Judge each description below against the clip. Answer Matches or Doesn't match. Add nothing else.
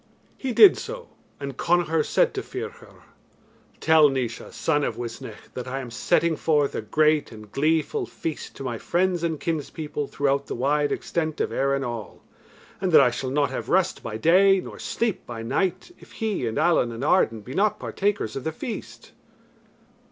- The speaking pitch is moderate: Matches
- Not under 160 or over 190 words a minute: Matches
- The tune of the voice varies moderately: Doesn't match